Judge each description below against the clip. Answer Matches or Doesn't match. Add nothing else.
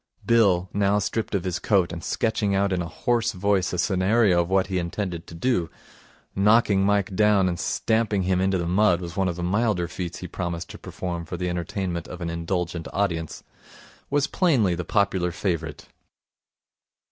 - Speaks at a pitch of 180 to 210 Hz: Doesn't match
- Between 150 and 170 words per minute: Doesn't match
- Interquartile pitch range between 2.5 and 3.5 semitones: Matches